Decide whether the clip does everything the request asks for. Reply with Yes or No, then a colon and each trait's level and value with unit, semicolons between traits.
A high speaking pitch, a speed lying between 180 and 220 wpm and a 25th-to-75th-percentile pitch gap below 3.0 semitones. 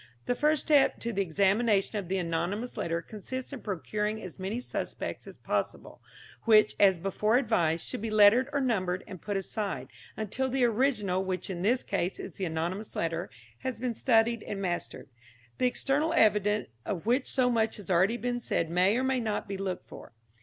No: high, 210 Hz; average, 190 wpm; average, 4.4 semitones